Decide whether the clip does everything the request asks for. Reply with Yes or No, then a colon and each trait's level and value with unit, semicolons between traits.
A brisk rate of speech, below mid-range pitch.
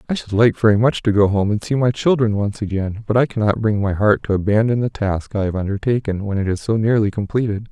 Yes: fast, 255 wpm; low, 105 Hz